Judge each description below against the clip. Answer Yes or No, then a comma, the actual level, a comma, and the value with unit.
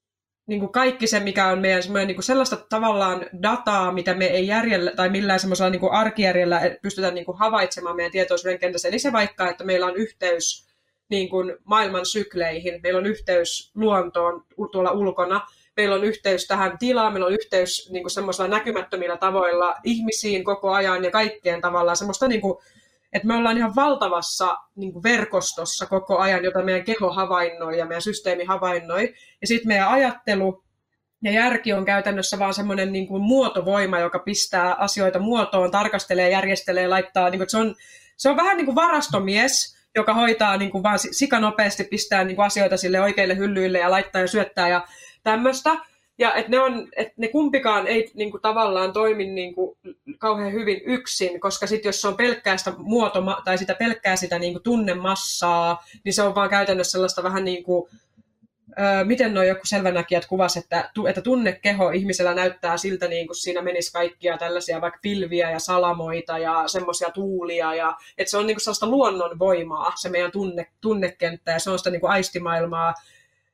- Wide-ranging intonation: No, average, 2.9 semitones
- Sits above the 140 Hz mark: Yes, high, 190 Hz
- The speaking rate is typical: No, fast, 170 wpm